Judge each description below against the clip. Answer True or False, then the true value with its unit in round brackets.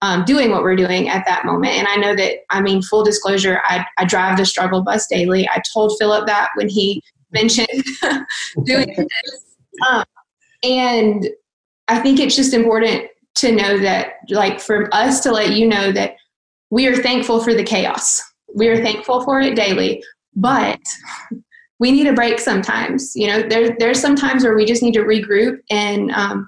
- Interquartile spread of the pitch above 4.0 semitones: False (3.6 semitones)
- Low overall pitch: False (225 Hz)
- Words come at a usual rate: True (185 wpm)